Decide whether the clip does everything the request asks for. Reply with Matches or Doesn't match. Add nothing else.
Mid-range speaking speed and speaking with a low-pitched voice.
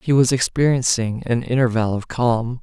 Matches